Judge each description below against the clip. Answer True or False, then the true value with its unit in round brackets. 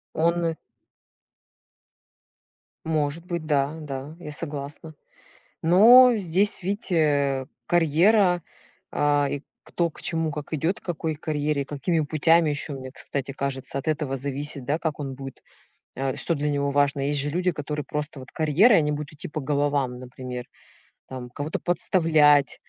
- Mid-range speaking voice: True (150 Hz)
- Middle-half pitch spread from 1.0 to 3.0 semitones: True (2.6 semitones)